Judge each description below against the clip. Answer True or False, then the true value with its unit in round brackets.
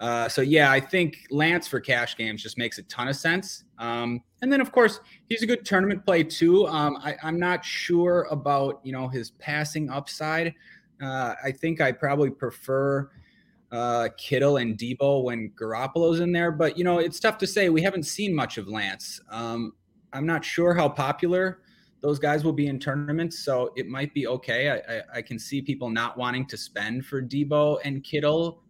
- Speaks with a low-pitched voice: False (145 Hz)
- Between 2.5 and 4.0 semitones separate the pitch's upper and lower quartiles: False (5.0 semitones)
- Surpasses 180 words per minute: True (200 wpm)